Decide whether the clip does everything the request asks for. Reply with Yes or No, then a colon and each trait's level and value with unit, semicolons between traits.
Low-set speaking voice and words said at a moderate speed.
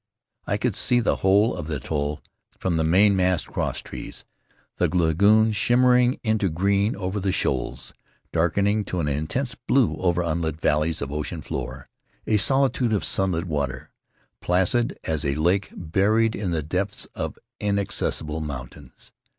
Yes: very low, 90 Hz; average, 145 wpm